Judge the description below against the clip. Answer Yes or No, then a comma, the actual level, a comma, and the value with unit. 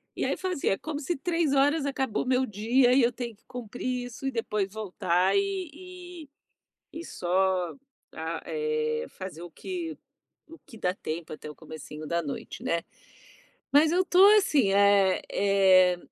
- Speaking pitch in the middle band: No, high, 245 Hz